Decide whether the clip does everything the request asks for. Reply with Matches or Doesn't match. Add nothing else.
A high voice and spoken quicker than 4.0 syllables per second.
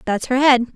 Matches